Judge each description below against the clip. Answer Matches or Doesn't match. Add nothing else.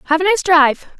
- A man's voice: Doesn't match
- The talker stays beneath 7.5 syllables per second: Matches